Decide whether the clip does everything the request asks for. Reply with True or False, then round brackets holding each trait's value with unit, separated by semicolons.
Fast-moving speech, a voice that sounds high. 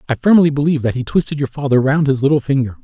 False (255 wpm; 140 Hz)